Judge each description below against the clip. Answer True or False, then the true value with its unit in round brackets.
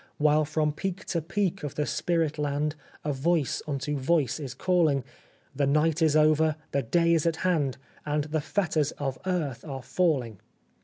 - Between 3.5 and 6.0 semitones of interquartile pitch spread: False (2.7 semitones)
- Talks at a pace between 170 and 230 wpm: True (175 wpm)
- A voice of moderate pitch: True (150 Hz)